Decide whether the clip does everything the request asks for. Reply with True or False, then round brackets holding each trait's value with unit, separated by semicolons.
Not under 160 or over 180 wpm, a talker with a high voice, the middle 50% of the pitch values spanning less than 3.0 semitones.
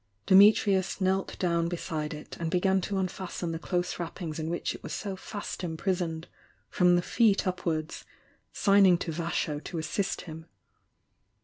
False (165 wpm; 175 Hz; 2.6 semitones)